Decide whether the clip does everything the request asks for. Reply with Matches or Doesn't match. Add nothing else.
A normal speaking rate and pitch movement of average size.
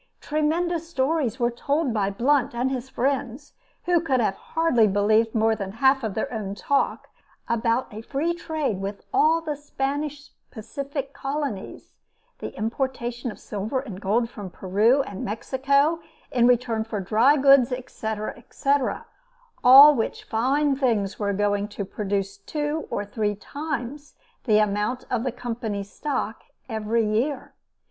Matches